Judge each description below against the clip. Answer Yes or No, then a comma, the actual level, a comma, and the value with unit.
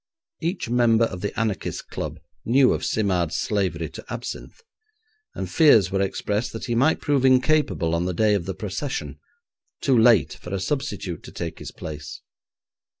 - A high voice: No, low, 110 Hz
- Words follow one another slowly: No, average, 165 wpm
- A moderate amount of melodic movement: No, wide, 5.8 semitones